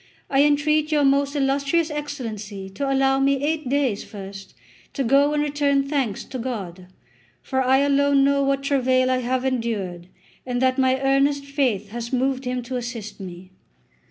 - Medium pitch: No, very high, 270 Hz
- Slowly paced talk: No, average, 165 wpm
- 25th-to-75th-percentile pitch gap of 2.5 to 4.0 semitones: Yes, average, 2.9 semitones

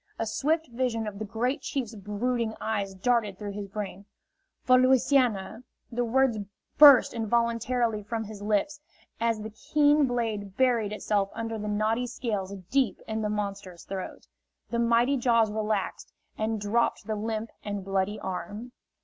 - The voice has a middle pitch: No, high, 220 Hz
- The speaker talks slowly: No, average, 150 wpm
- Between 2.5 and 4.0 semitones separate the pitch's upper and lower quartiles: Yes, average, 2.9 semitones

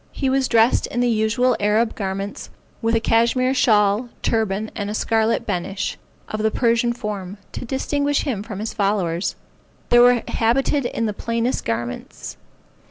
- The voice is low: No, high, 225 Hz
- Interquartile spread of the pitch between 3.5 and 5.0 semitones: No, average, 2.9 semitones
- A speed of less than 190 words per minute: Yes, average, 160 wpm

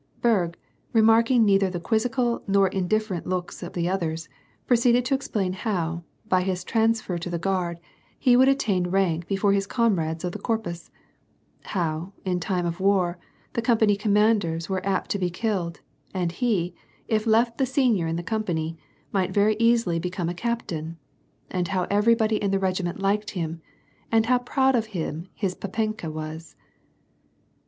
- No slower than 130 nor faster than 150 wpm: No, average, 170 wpm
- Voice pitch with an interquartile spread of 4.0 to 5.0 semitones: Yes, average, 4.3 semitones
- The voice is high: Yes, high, 195 Hz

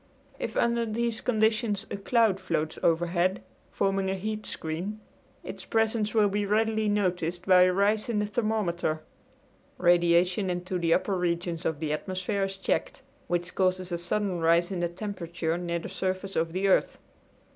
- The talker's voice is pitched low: No, medium, 185 Hz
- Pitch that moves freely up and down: No, average, 3.3 semitones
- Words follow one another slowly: No, average, 165 wpm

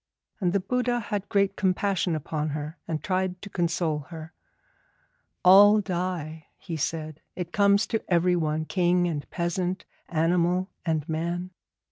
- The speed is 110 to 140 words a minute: Yes, slow, 135 wpm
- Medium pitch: Yes, medium, 175 Hz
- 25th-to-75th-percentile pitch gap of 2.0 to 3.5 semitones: Yes, average, 2.9 semitones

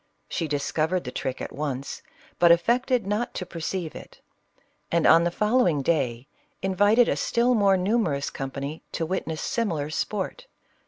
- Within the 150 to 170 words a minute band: Yes, average, 155 wpm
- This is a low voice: No, medium, 170 Hz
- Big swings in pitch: Yes, wide, 5.9 semitones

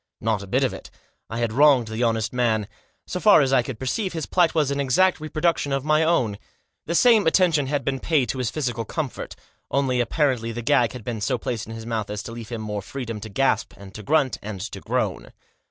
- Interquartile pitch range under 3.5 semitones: No, average, 4.8 semitones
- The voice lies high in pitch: No, low, 125 Hz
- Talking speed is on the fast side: Yes, fast, 235 wpm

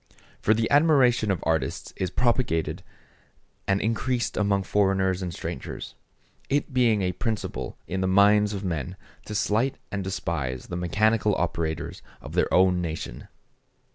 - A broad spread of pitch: No, average, 4.0 semitones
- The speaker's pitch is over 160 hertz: No, low, 100 Hz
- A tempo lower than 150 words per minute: Yes, average, 140 wpm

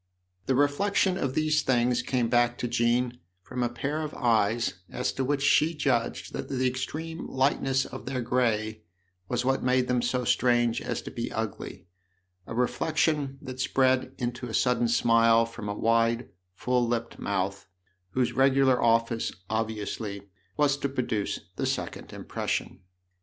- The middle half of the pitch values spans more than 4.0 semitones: No, narrow, 2.5 semitones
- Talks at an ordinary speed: Yes, average, 155 wpm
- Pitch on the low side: Yes, low, 125 Hz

